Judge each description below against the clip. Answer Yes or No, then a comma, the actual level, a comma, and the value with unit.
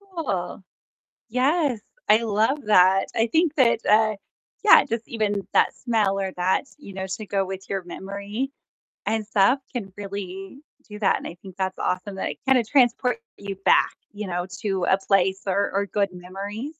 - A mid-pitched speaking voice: No, high, 200 Hz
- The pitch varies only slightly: No, average, 3.3 semitones